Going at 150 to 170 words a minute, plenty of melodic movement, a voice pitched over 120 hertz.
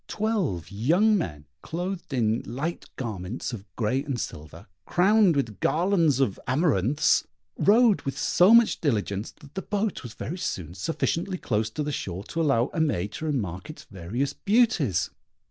Yes: average, 155 wpm; wide, 8.9 semitones; medium, 140 Hz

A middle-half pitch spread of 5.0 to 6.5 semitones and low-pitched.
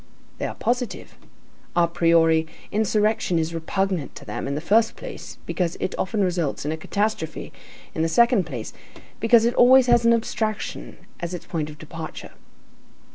No: wide, 5.5 semitones; medium, 180 Hz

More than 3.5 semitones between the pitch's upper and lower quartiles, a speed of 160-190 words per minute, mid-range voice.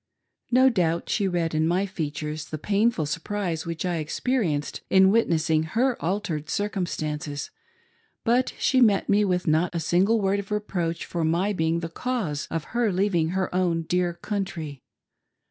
Yes: average, 4.1 semitones; average, 165 wpm; medium, 175 Hz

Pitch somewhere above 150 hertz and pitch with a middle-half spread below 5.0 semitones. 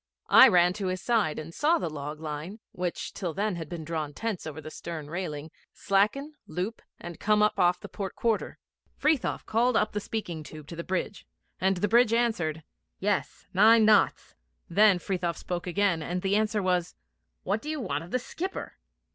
Yes: medium, 185 Hz; average, 4.4 semitones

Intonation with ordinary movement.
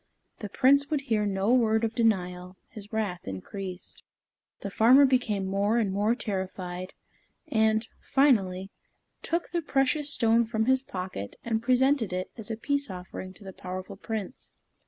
Yes: average, 4.8 semitones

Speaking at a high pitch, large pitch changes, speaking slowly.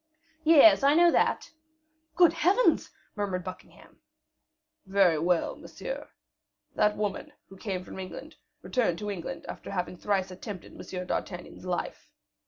Yes: high, 195 Hz; wide, 7.1 semitones; slow, 130 wpm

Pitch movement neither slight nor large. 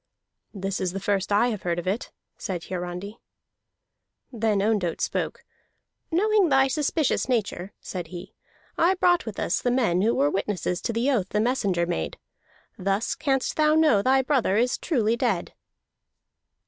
No: wide, 5.9 semitones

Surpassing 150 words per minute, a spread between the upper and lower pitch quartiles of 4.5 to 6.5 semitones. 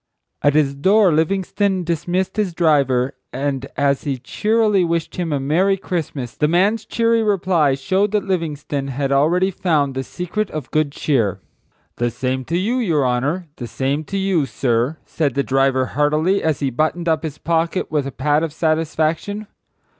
Yes: average, 170 wpm; average, 5.0 semitones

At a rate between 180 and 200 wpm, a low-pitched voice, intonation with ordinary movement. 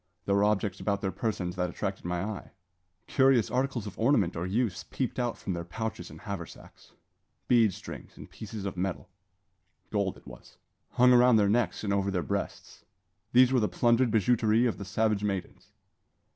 Yes: average, 185 wpm; low, 105 Hz; average, 3.7 semitones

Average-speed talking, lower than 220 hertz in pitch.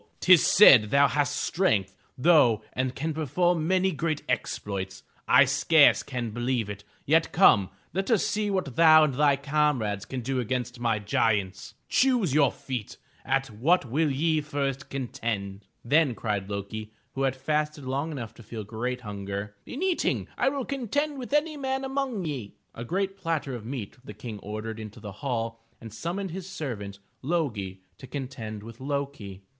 Yes: average, 170 wpm; low, 135 Hz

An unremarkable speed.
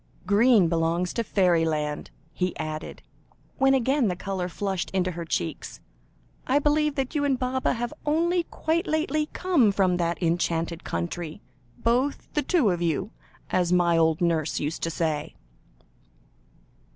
Yes: average, 145 wpm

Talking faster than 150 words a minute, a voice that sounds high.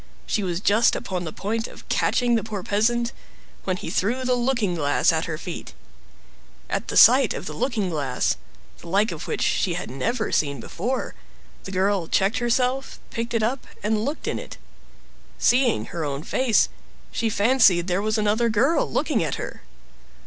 Yes: average, 180 wpm; high, 215 Hz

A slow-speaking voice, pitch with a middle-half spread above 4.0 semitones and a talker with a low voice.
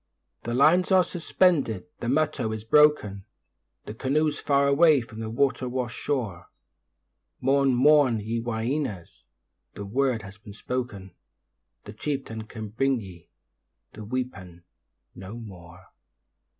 Yes: slow, 125 wpm; average, 4.9 semitones; low, 120 Hz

